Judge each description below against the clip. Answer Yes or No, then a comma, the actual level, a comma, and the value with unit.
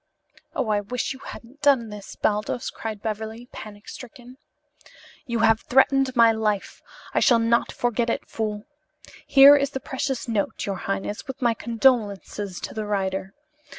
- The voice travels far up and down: No, average, 3.2 semitones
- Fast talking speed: No, average, 155 wpm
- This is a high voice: Yes, high, 225 Hz